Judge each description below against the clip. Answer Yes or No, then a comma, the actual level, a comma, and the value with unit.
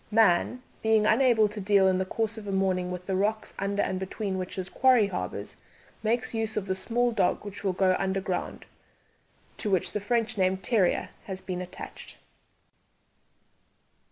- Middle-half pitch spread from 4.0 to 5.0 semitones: No, average, 2.7 semitones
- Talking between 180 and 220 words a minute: No, average, 170 wpm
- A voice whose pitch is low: No, high, 200 Hz